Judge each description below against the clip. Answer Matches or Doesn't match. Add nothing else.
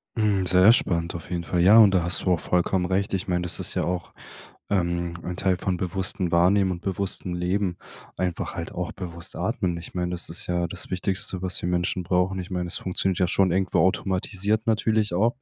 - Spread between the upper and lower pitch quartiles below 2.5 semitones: Matches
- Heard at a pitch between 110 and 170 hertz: Doesn't match